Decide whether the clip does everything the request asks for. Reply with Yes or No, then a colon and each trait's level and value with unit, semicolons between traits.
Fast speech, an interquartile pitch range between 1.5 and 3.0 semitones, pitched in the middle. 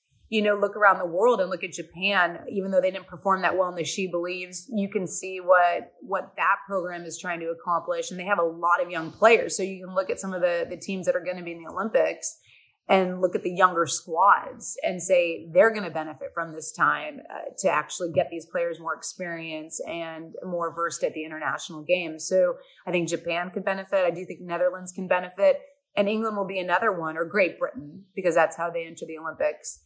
Yes: fast, 235 wpm; narrow, 2.4 semitones; medium, 180 Hz